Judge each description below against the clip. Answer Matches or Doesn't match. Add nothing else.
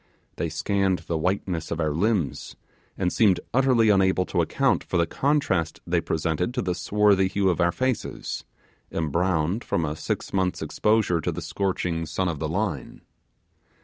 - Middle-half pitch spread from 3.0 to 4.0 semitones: Matches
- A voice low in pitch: Matches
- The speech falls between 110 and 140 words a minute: Doesn't match